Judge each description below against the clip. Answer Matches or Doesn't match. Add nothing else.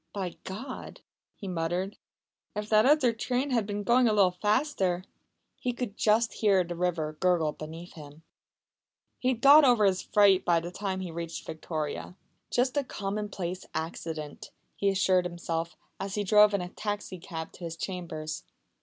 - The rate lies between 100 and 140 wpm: Doesn't match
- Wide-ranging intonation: Doesn't match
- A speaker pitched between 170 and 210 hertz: Matches